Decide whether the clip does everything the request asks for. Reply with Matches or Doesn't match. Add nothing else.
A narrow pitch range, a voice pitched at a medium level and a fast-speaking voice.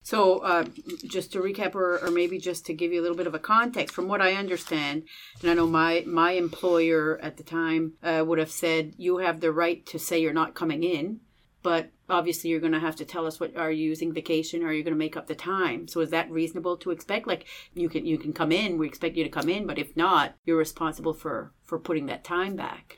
Matches